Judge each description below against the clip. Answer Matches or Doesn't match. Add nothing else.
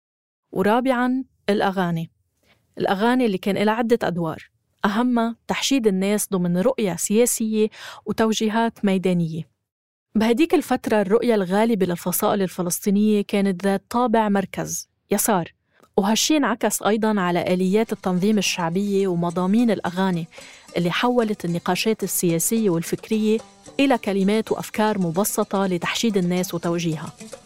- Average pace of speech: Matches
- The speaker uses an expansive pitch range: Doesn't match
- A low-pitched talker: Doesn't match